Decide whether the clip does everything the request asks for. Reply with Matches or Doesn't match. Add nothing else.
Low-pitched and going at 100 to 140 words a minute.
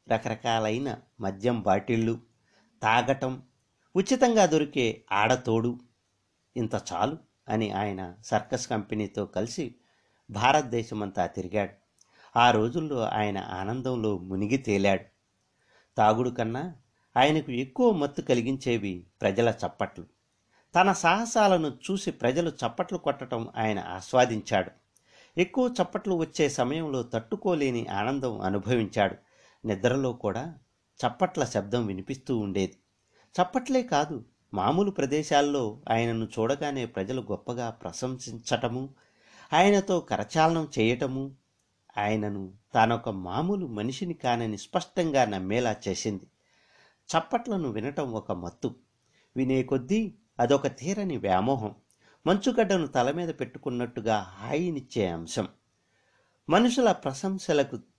Doesn't match